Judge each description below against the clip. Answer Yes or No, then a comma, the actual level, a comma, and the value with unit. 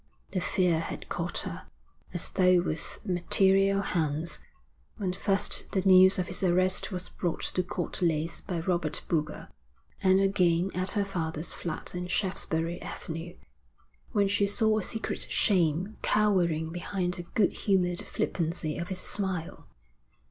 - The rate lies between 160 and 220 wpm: No, average, 145 wpm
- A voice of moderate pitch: Yes, medium, 180 Hz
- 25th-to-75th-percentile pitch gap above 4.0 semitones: No, narrow, 2.4 semitones